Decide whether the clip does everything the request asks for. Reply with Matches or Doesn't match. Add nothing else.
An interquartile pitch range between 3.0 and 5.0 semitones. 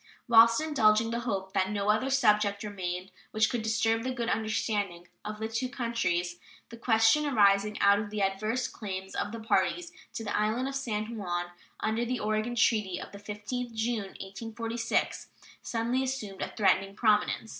Doesn't match